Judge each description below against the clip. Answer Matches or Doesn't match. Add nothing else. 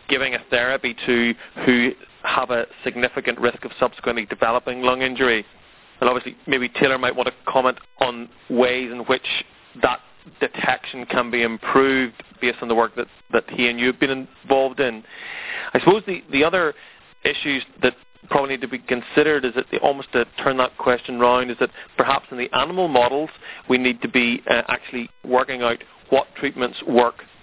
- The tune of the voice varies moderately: Doesn't match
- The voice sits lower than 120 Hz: Doesn't match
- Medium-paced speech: Matches